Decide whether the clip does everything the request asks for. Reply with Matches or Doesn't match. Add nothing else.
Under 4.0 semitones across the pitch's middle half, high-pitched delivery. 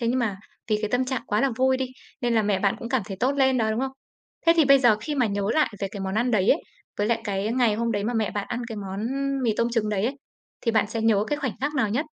Matches